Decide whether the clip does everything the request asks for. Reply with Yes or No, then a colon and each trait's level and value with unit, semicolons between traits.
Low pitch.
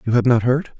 Yes: low, 125 Hz